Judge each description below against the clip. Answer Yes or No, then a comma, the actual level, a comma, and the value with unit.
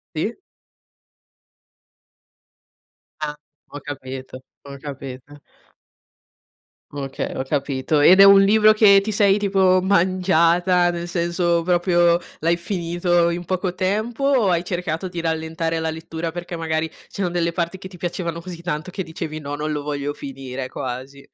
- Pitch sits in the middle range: Yes, medium, 170 Hz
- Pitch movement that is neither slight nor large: Yes, average, 3.4 semitones